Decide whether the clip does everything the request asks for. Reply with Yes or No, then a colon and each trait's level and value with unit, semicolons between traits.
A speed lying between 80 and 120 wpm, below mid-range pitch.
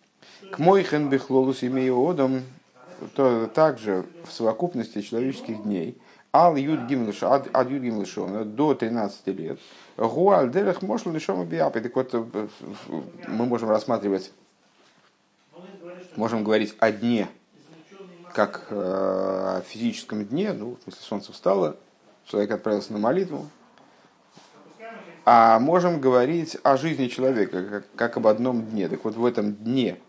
Yes: slow, 110 wpm; low, 125 Hz